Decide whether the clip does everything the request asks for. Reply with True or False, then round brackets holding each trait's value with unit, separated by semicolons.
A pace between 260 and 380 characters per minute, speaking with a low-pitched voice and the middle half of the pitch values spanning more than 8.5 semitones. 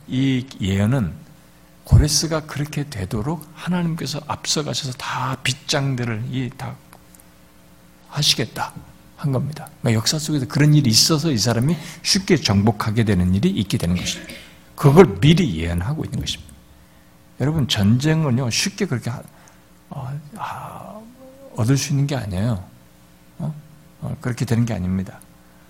True (280 characters per minute; 125 Hz; 9.0 semitones)